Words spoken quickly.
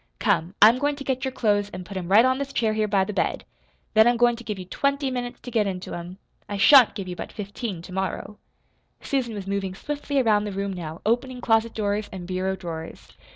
Yes: fast, 230 wpm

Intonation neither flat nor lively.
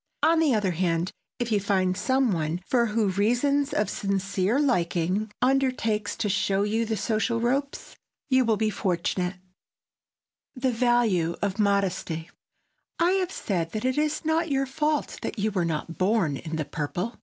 No: wide, 5.7 semitones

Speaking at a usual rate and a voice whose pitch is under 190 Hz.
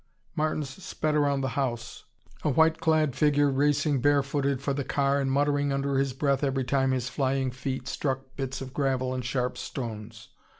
Yes: average, 180 wpm; low, 135 Hz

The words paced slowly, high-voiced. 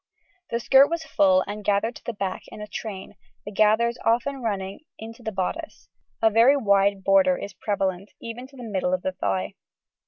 No: average, 190 wpm; high, 210 Hz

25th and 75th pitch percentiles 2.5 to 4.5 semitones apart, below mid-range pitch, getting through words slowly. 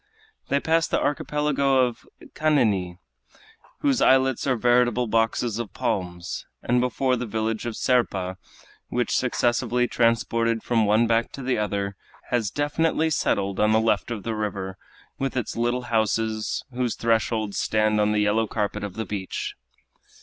No: average, 2.8 semitones; low, 115 Hz; average, 150 wpm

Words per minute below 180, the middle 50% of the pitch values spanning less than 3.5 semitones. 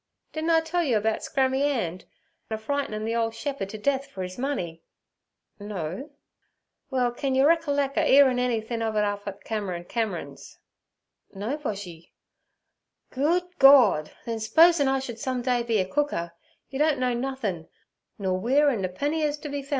No: average, 170 wpm; wide, 5.5 semitones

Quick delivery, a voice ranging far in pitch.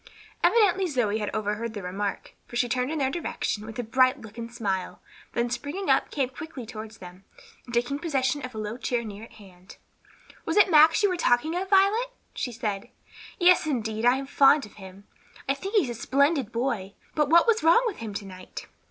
Yes: fast, 210 wpm; wide, 6.3 semitones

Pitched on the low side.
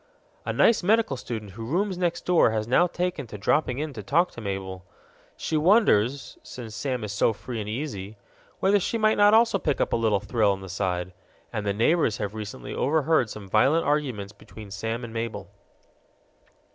Yes: low, 120 Hz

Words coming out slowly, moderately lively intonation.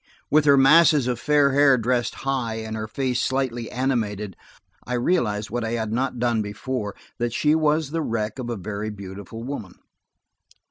No: average, 170 wpm; average, 3.9 semitones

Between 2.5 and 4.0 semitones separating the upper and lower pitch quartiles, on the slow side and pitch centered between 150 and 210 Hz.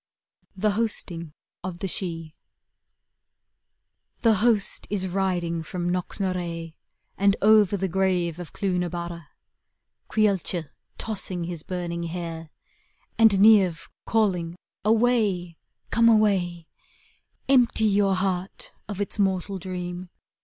Yes: average, 2.9 semitones; slow, 110 wpm; medium, 185 Hz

